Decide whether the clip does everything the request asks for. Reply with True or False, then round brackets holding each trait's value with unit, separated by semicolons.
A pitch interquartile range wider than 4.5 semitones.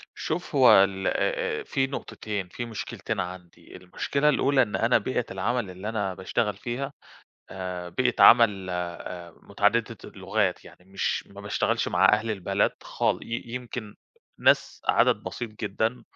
True (4.9 semitones)